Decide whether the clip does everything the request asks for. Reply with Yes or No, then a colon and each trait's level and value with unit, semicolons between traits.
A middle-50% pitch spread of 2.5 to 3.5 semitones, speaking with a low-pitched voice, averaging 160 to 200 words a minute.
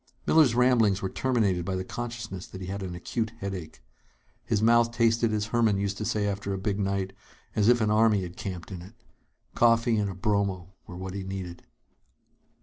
Yes: average, 3.2 semitones; low, 100 Hz; average, 195 wpm